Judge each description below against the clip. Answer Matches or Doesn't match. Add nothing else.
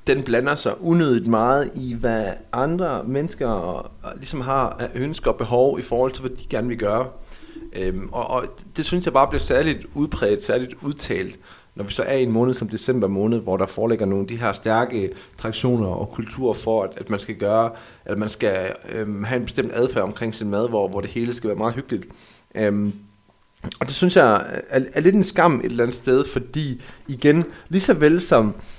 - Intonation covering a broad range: Doesn't match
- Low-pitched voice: Matches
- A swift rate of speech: Doesn't match